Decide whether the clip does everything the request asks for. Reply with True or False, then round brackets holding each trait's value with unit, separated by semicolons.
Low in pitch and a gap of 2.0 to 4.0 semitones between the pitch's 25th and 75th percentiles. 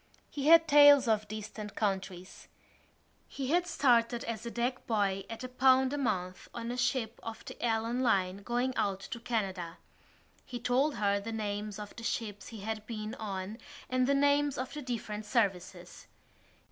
False (225 Hz; 3.7 semitones)